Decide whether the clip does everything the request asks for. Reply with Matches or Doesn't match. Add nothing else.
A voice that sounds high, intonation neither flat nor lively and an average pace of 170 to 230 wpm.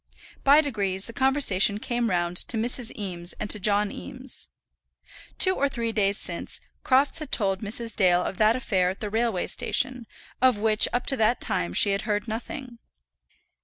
Matches